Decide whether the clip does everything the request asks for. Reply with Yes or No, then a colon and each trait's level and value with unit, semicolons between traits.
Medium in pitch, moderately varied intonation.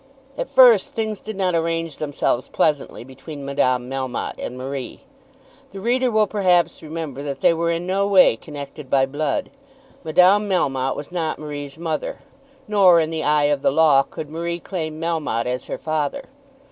Yes: medium, 160 Hz; average, 4.5 semitones